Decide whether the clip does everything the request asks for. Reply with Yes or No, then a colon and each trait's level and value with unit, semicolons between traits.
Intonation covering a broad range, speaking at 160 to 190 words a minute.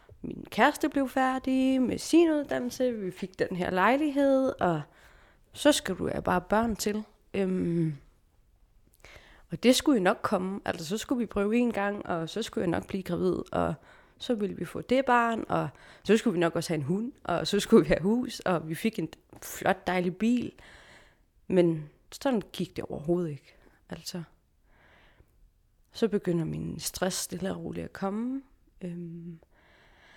Yes: wide, 5.8 semitones; average, 175 wpm